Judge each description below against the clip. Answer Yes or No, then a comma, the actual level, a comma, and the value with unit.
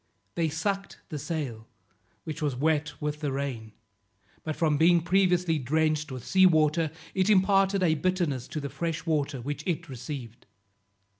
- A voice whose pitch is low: No, medium, 155 Hz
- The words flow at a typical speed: Yes, average, 155 wpm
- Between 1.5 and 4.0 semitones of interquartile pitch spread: Yes, average, 3.5 semitones